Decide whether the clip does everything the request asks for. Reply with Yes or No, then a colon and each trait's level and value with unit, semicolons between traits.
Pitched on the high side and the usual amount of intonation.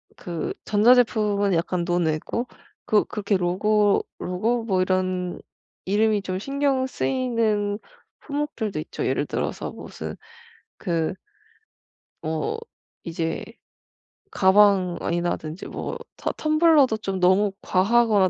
Yes: high, 205 Hz; average, 4.2 semitones